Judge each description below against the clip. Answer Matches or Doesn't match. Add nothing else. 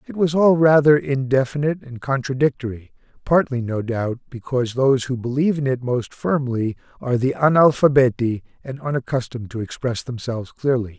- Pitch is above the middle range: Doesn't match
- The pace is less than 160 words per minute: Matches